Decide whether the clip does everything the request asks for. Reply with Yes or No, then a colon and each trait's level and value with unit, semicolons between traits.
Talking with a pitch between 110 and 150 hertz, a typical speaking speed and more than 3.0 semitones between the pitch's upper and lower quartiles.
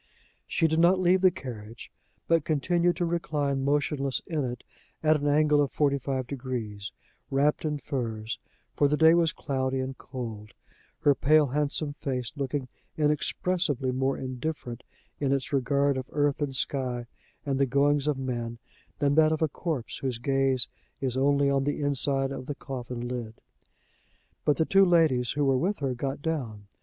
No: medium, 140 Hz; average, 170 wpm; average, 2.7 semitones